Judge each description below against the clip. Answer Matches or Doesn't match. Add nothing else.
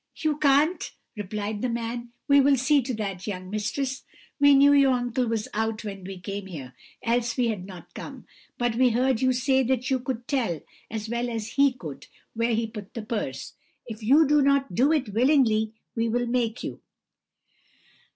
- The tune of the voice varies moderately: Matches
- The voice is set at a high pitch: Matches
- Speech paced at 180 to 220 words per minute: Matches